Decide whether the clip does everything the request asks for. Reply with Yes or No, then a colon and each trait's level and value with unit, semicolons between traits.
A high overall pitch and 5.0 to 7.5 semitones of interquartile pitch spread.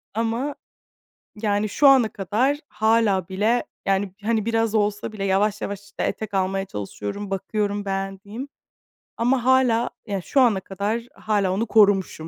No: high, 205 Hz; average, 2.8 semitones